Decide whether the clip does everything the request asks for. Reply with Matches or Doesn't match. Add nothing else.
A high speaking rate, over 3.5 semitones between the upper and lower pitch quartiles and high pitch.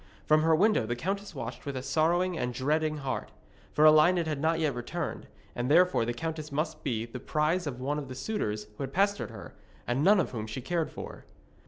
Doesn't match